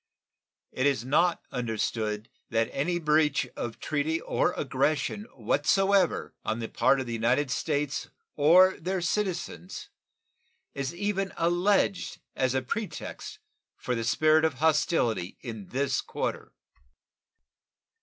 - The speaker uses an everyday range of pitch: No, wide, 5.9 semitones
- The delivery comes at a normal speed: No, slow, 120 wpm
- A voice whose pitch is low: No, medium, 145 Hz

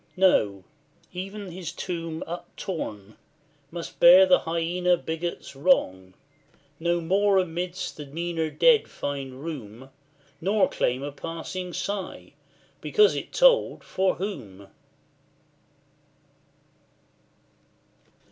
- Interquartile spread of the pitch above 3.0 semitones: Yes, average, 4.6 semitones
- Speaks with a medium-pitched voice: Yes, medium, 170 Hz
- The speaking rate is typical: No, slow, 95 wpm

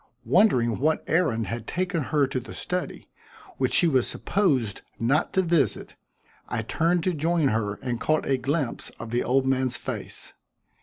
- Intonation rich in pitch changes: Yes, wide, 5.8 semitones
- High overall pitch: No, low, 135 Hz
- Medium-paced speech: Yes, average, 165 wpm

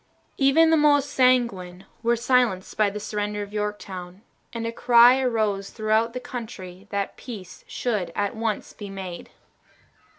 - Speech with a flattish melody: No, average, 3.7 semitones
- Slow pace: No, average, 145 wpm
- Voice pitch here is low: No, high, 215 Hz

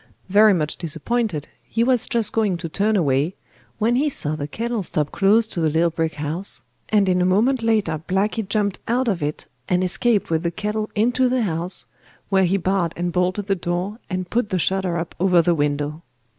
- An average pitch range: Yes, average, 4.5 semitones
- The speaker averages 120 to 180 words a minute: No, average, 200 wpm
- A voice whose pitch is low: No, medium, 185 Hz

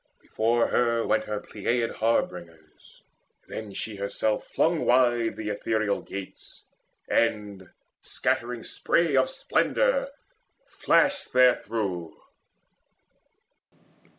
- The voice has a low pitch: Yes, low, 115 Hz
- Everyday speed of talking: No, slow, 95 wpm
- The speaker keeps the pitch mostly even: No, average, 3.3 semitones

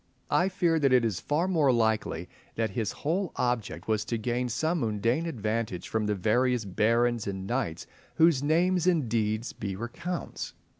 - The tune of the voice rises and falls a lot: Yes, wide, 6.5 semitones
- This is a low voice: Yes, low, 120 Hz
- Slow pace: No, average, 165 wpm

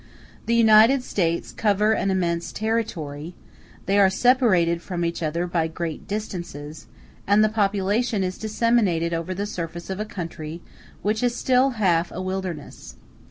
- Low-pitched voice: No, high, 190 Hz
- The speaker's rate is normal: Yes, average, 155 wpm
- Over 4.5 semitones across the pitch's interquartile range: No, average, 4.2 semitones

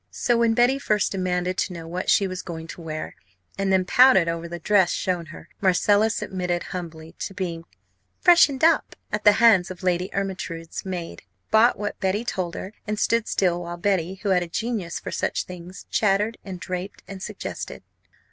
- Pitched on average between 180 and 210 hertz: Yes, medium, 185 Hz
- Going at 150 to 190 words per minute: Yes, average, 185 wpm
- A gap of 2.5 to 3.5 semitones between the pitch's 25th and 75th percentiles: Yes, average, 3.2 semitones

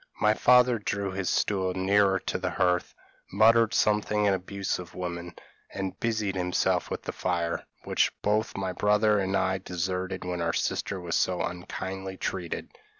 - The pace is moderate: Yes, average, 165 wpm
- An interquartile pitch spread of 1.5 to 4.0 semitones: Yes, narrow, 2.4 semitones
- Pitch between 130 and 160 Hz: No, very low, 95 Hz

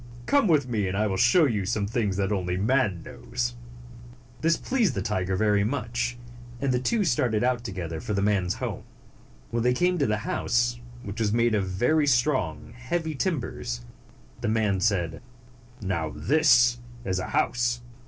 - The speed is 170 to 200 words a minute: Yes, average, 180 wpm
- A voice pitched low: Yes, low, 115 Hz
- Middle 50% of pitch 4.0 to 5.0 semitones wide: Yes, average, 4.4 semitones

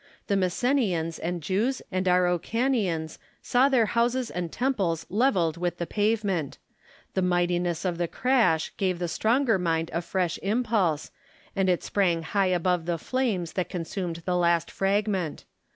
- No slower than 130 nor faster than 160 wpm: Yes, average, 150 wpm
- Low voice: No, medium, 180 Hz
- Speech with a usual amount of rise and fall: Yes, average, 4.1 semitones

